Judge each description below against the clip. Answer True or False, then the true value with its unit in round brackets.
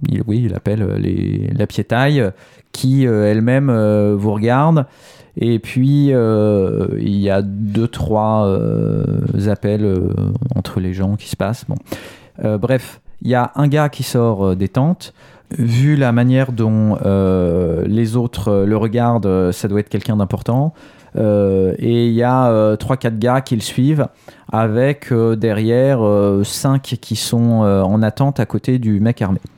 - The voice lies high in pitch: False (115 Hz)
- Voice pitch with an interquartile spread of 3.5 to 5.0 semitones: True (3.8 semitones)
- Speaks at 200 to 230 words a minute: False (170 wpm)